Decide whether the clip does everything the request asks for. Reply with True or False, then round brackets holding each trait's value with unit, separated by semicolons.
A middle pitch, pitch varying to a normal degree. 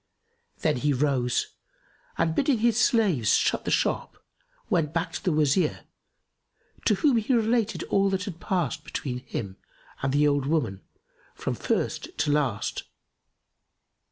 False (155 Hz; 6.4 semitones)